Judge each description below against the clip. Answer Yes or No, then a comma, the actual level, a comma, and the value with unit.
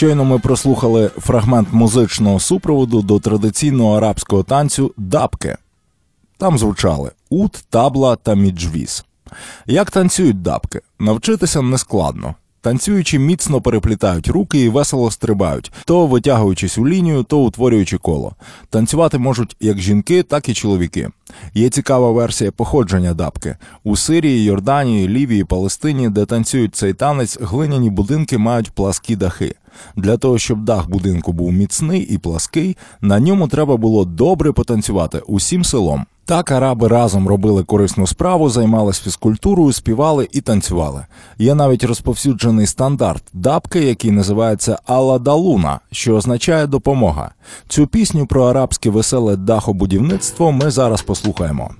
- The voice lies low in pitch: Yes, low, 115 Hz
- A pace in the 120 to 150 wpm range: Yes, average, 130 wpm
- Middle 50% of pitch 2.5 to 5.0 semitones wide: No, wide, 5.4 semitones